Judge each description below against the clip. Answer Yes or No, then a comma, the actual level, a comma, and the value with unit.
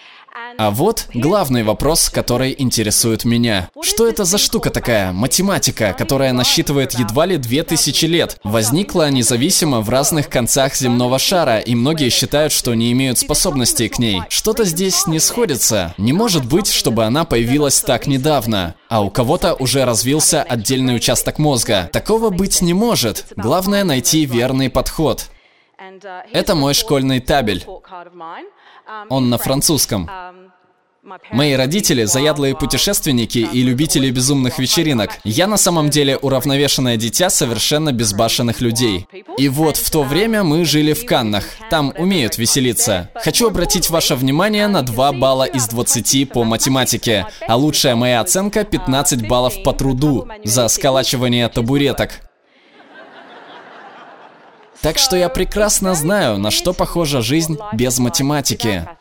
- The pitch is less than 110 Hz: No, medium, 140 Hz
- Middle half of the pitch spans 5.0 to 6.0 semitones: Yes, wide, 5.6 semitones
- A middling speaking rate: Yes, average, 135 wpm